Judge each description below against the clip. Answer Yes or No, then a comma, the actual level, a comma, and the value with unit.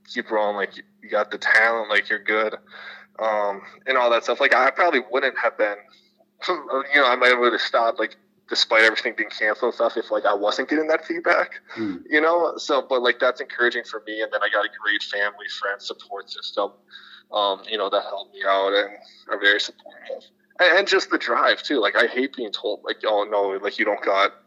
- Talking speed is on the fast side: Yes, fast, 215 wpm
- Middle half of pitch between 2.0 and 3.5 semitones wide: No, average, 4.6 semitones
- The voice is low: Yes, low, 110 Hz